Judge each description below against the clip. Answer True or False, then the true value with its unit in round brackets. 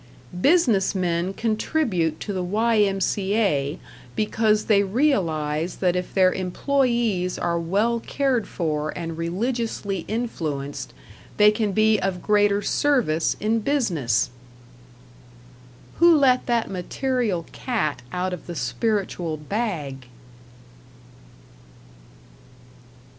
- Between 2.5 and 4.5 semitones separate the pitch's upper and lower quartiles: False (5.2 semitones)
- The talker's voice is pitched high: True (195 Hz)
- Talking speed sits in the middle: False (100 wpm)